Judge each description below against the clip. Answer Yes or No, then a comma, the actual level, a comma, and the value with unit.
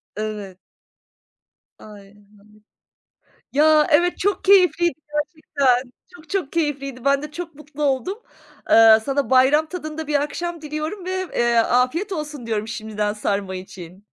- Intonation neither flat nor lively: No, wide, 6.1 semitones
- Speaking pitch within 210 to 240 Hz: No, very high, 280 Hz